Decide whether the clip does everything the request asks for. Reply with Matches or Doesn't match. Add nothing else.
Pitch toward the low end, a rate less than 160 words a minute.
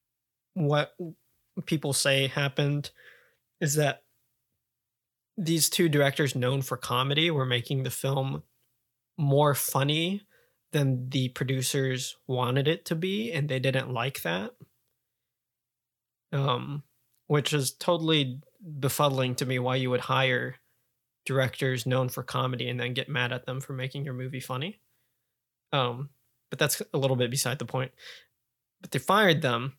Matches